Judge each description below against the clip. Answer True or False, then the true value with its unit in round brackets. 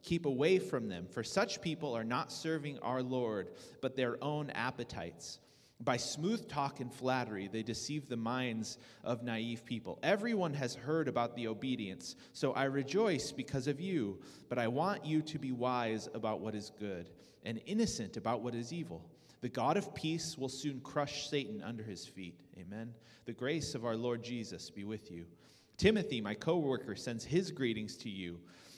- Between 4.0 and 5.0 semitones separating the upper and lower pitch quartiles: True (4.5 semitones)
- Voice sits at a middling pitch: False (125 Hz)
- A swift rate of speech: False (180 wpm)